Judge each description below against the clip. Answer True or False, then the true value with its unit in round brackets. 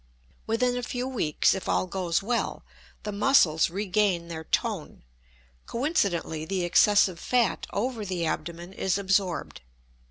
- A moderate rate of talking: False (130 wpm)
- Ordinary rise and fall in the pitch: True (4.6 semitones)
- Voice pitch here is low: False (195 Hz)